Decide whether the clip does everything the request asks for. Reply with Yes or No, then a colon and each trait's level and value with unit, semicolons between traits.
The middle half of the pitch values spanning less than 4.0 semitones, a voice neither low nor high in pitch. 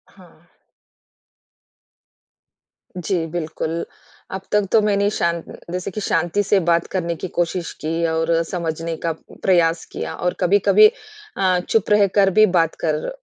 Yes: average, 2.9 semitones; medium, 175 Hz